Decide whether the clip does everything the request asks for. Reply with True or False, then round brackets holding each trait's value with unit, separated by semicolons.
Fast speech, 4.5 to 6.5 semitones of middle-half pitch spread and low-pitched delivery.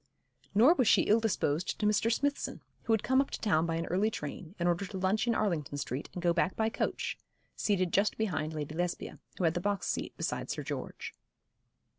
False (215 wpm; 4.8 semitones; 185 Hz)